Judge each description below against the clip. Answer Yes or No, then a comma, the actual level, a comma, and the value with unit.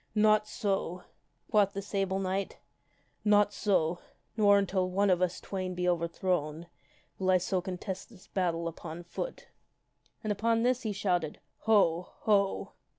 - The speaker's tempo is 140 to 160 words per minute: Yes, average, 155 wpm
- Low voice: No, high, 190 Hz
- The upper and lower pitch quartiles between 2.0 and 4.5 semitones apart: Yes, narrow, 2.5 semitones